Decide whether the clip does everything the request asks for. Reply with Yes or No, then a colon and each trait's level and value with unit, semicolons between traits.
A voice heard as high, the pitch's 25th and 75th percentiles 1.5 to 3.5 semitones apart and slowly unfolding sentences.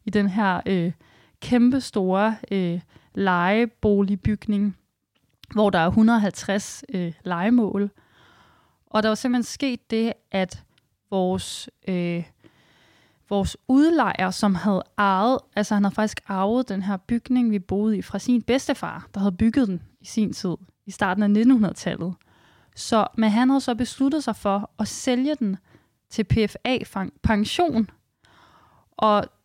Yes: high, 210 Hz; average, 3.2 semitones; slow, 135 wpm